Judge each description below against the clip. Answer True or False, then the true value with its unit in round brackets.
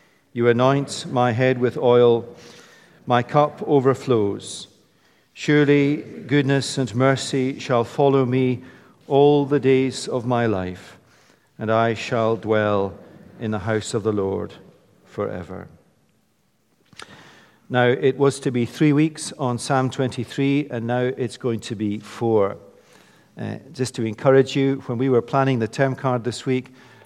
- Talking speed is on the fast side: False (140 wpm)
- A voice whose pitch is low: True (130 Hz)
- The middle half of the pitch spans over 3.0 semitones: False (2.6 semitones)